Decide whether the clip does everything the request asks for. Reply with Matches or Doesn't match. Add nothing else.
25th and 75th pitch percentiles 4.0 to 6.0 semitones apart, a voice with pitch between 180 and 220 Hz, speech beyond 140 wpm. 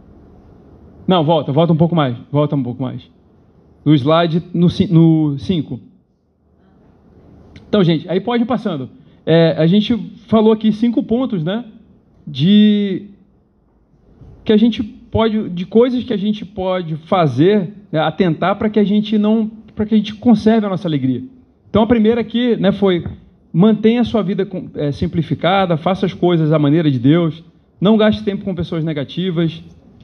Matches